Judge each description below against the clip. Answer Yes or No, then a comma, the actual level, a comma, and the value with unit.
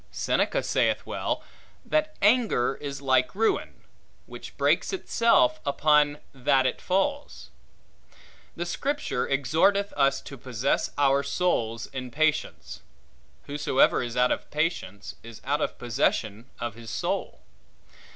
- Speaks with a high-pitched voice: No, medium, 140 Hz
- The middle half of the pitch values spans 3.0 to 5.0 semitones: No, wide, 5.6 semitones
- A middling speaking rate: No, slow, 120 wpm